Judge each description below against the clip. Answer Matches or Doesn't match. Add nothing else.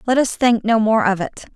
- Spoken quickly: Matches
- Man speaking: Doesn't match